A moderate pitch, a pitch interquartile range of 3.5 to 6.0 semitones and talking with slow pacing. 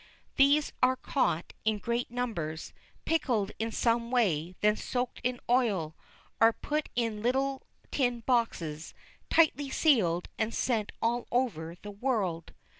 No: high, 235 Hz; average, 3.8 semitones; slow, 130 wpm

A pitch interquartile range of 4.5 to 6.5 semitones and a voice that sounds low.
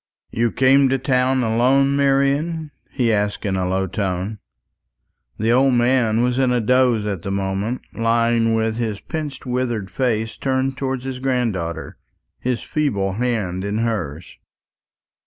No: average, 3.9 semitones; low, 120 Hz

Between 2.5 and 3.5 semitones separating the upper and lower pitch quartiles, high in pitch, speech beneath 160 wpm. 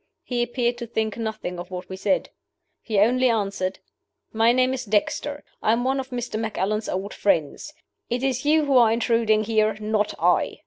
No: average, 2.9 semitones; high, 225 Hz; average, 185 wpm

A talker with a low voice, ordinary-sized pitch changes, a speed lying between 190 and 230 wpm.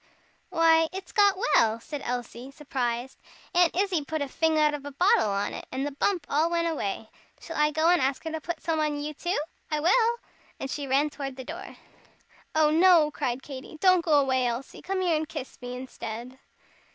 No: very high, 300 Hz; average, 4.0 semitones; fast, 205 wpm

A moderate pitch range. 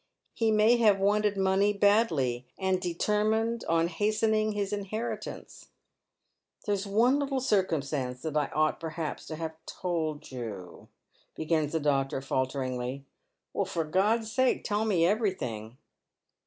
No: wide, 6.1 semitones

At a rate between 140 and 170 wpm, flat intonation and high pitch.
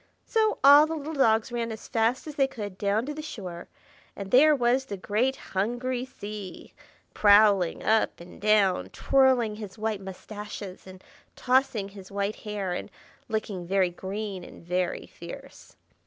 No: average, 155 wpm; average, 4.5 semitones; high, 215 Hz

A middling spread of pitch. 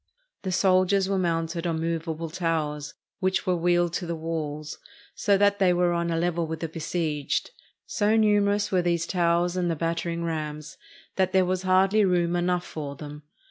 No: narrow, 2.3 semitones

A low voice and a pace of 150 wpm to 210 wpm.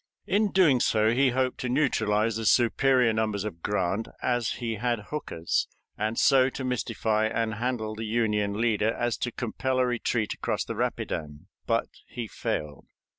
Yes: low, 115 Hz; average, 165 wpm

